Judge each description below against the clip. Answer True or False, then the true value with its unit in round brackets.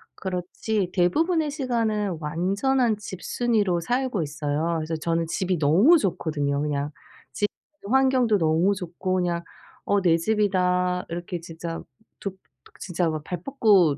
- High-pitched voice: False (180 Hz)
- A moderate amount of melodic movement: True (4.4 semitones)